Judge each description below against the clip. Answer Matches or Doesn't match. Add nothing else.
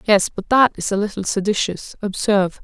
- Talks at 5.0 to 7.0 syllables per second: Matches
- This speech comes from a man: Doesn't match